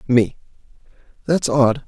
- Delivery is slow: Yes, slow, 95 wpm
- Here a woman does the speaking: No, male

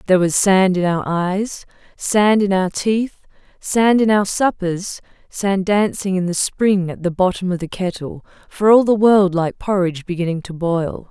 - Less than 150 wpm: No, average, 185 wpm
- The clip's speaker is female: Yes, female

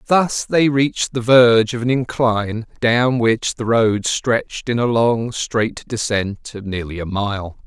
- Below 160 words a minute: No, average, 170 wpm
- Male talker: Yes, male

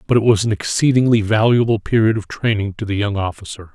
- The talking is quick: Yes, fast, 210 wpm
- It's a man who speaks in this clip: Yes, male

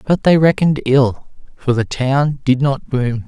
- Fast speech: No, average, 185 wpm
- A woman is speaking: No, male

